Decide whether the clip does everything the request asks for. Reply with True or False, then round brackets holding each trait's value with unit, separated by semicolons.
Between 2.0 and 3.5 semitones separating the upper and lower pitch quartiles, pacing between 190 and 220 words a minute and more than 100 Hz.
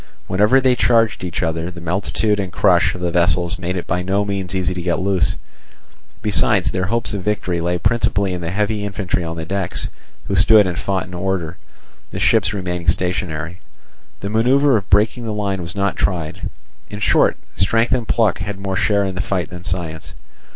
False (2.7 semitones; 195 wpm; 95 Hz)